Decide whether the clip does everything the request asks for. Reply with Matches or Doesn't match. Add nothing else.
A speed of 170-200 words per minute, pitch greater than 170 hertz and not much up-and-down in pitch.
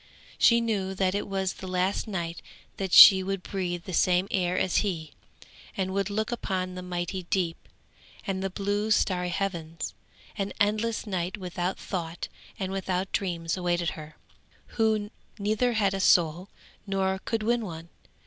Doesn't match